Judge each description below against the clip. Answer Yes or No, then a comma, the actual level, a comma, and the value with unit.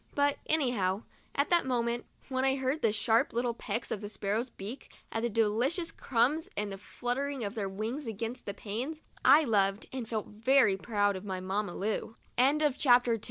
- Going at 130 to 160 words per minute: No, average, 170 wpm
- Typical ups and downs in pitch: Yes, average, 4.3 semitones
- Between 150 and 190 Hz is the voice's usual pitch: No, high, 230 Hz